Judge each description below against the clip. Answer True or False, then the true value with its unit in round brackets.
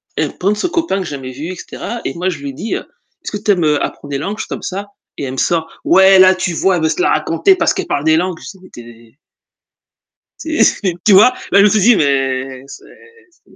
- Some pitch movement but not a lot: False (6.0 semitones)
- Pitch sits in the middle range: True (180 Hz)